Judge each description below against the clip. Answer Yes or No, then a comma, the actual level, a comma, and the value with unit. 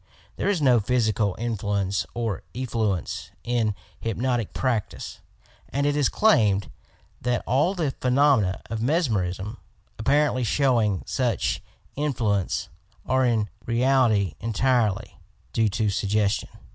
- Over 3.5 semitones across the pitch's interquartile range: Yes, average, 4.0 semitones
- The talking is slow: Yes, slow, 115 wpm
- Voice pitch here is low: Yes, low, 115 Hz